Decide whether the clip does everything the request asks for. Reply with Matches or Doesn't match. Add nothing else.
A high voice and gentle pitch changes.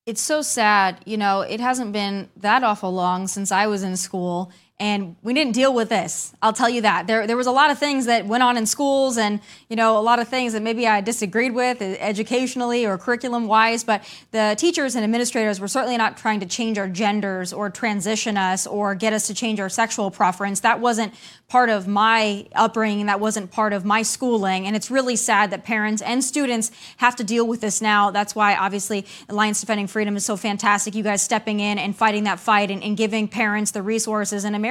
Matches